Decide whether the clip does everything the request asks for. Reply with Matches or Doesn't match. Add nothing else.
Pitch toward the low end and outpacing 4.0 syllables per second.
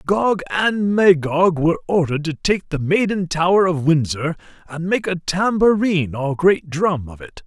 Doesn't match